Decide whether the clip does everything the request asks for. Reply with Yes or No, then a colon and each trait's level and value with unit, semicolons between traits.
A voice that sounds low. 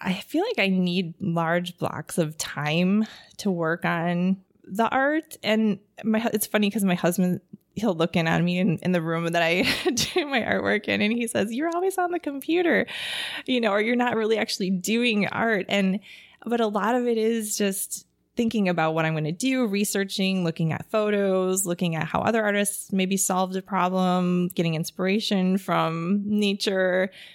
No: high, 195 Hz